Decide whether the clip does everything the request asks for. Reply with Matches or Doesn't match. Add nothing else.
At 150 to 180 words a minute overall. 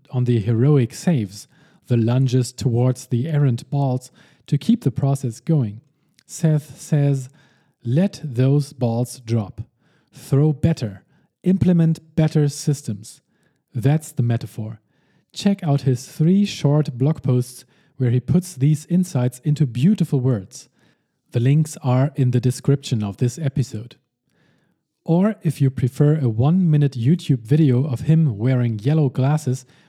Doesn't match